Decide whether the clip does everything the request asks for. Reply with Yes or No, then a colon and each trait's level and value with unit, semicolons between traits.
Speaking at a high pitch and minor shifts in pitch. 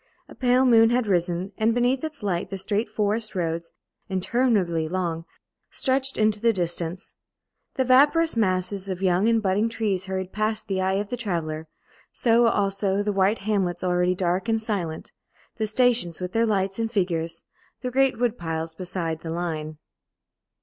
No: high, 195 Hz; average, 4.3 semitones